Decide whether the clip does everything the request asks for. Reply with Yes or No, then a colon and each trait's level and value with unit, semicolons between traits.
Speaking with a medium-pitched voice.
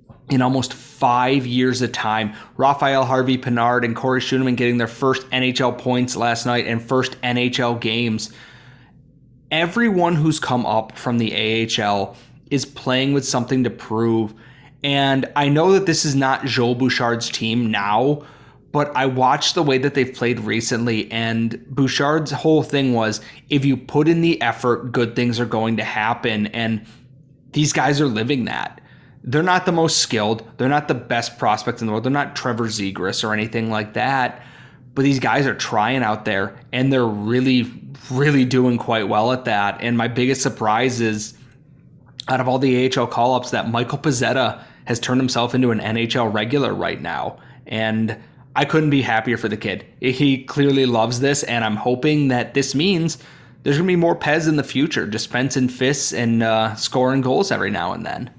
No: low, 125 Hz